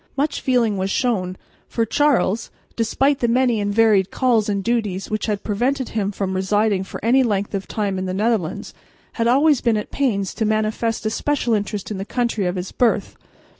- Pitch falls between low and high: No, high, 215 Hz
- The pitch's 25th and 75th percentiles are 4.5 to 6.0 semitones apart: No, average, 3.3 semitones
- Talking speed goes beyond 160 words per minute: Yes, average, 195 wpm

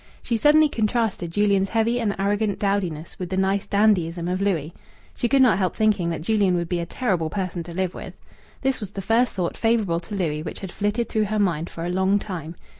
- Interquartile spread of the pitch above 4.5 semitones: No, average, 3.8 semitones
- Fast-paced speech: Yes, fast, 220 wpm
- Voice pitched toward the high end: Yes, high, 195 Hz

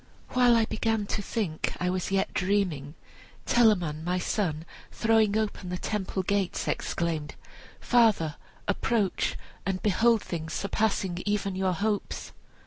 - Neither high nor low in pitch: No, high, 195 Hz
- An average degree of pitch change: Yes, average, 3.6 semitones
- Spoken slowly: Yes, slow, 130 wpm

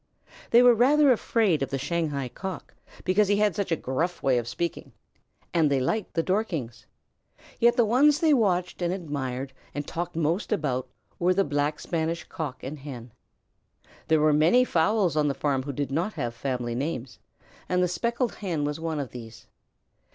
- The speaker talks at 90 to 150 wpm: No, average, 180 wpm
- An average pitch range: No, wide, 6.1 semitones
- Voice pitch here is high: No, medium, 160 Hz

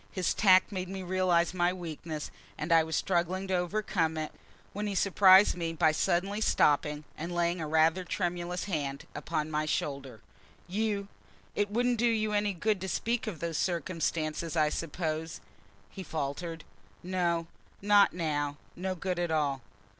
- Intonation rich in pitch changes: No, average, 3.2 semitones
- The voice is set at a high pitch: No, medium, 175 Hz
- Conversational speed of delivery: Yes, average, 160 wpm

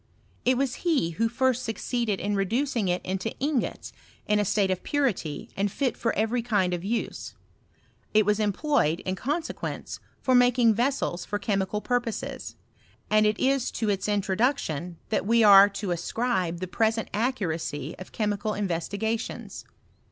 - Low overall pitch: No, high, 215 Hz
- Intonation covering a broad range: No, average, 4.2 semitones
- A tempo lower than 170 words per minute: Yes, average, 160 wpm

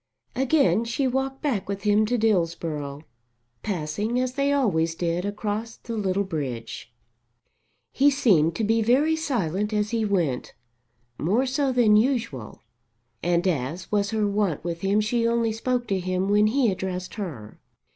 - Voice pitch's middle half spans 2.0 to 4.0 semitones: No, average, 5.2 semitones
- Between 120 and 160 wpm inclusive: Yes, average, 155 wpm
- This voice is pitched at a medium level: No, high, 210 Hz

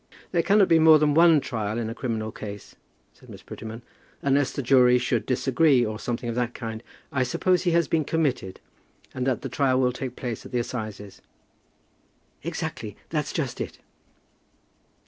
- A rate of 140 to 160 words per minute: No, average, 175 wpm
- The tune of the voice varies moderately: Yes, average, 4.3 semitones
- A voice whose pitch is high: No, low, 125 Hz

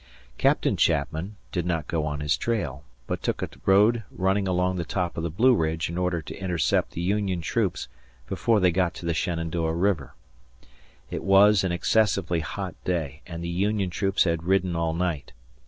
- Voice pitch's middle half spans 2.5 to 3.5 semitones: Yes, average, 2.8 semitones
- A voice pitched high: No, very low, 90 Hz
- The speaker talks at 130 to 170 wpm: No, average, 185 wpm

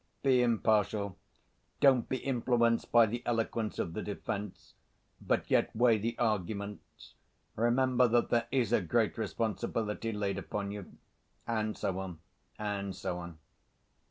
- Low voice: Yes, low, 110 Hz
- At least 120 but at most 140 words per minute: Yes, slow, 135 wpm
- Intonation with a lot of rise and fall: No, average, 2.8 semitones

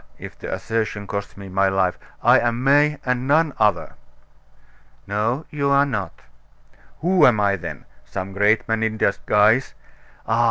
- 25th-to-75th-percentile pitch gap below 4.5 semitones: No, average, 5.0 semitones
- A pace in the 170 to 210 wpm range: No, average, 150 wpm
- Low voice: Yes, low, 110 Hz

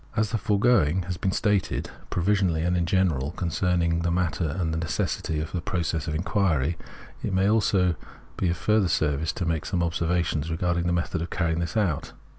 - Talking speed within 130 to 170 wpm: No, average, 195 wpm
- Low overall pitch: Yes, very low, 85 Hz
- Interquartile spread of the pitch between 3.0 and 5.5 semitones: No, narrow, 2.5 semitones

